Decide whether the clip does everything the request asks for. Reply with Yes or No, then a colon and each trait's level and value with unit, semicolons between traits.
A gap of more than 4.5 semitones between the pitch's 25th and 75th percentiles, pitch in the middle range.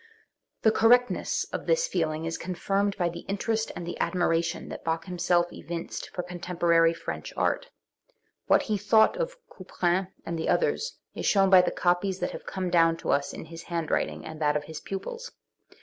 No: average, 3.3 semitones; medium, 180 Hz